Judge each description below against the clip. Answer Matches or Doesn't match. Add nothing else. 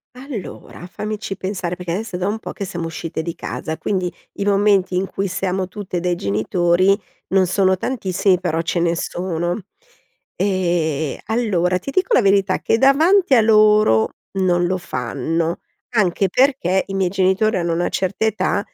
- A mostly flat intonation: Doesn't match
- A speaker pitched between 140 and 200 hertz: Matches